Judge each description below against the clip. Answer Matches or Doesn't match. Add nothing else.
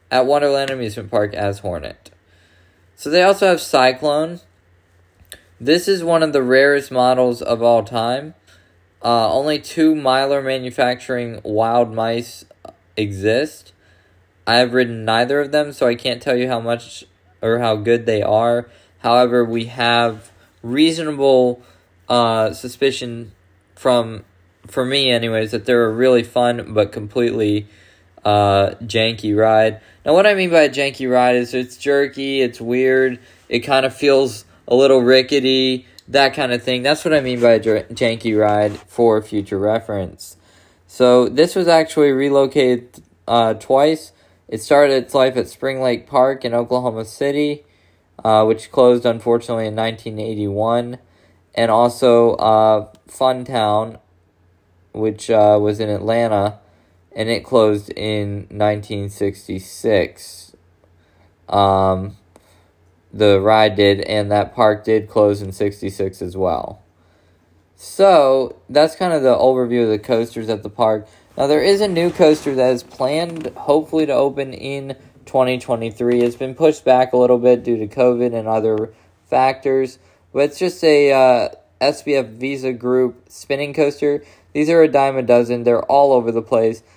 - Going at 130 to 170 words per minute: Matches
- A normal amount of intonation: Matches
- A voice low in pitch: Matches